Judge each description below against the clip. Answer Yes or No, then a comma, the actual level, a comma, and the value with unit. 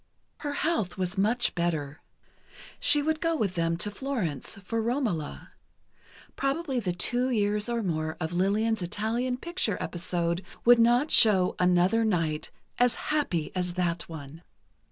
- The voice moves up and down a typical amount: No, wide, 5.9 semitones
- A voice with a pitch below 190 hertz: No, high, 205 Hz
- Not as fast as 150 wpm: Yes, average, 140 wpm